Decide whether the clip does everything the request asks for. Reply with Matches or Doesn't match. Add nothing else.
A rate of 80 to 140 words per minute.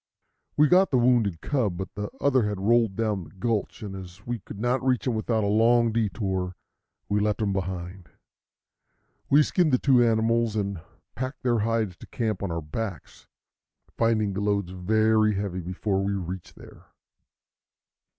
Doesn't match